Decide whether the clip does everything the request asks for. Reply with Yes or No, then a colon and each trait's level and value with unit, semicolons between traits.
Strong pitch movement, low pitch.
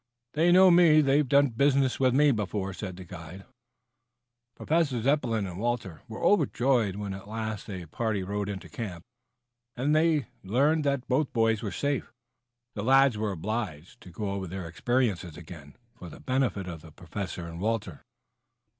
Yes: wide, 5.9 semitones; low, 110 Hz